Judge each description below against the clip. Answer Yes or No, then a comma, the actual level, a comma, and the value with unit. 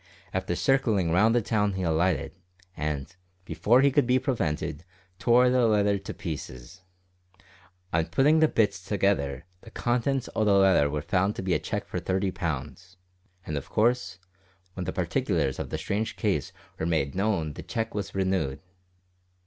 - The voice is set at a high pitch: No, very low, 95 Hz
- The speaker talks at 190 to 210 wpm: No, average, 165 wpm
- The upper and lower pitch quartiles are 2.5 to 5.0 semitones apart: No, wide, 5.6 semitones